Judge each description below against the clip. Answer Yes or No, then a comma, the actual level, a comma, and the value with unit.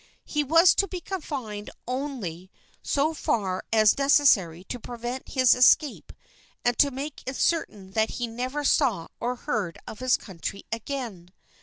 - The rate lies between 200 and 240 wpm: No, average, 150 wpm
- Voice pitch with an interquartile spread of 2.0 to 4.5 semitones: No, average, 5.2 semitones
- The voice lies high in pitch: Yes, very high, 250 Hz